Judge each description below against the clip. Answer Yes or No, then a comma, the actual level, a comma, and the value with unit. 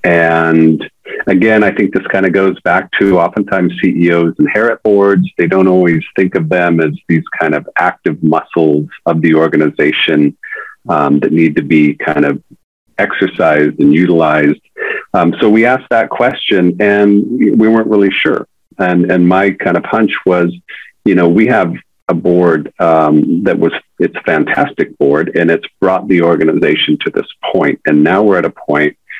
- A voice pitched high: No, very low, 85 Hz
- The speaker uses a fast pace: No, average, 175 wpm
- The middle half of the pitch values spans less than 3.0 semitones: No, average, 3.5 semitones